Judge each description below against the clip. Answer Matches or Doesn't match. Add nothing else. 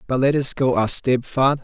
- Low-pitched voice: Matches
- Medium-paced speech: Doesn't match